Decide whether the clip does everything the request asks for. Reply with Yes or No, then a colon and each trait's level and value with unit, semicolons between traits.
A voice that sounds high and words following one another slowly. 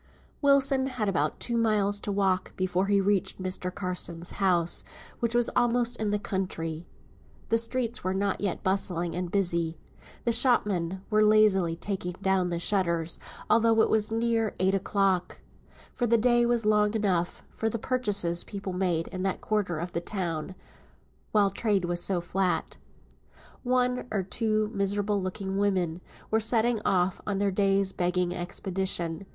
No: high, 195 Hz; average, 155 wpm